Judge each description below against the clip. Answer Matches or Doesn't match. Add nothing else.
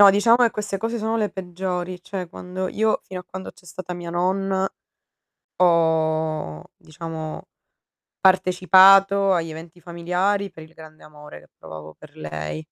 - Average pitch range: Matches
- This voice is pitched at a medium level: Matches